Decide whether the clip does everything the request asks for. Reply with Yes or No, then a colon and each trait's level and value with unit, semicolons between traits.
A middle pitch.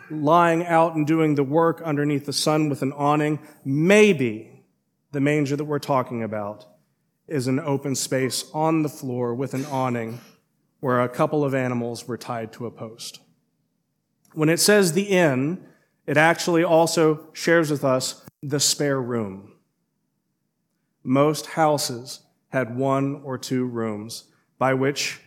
Yes: medium, 145 Hz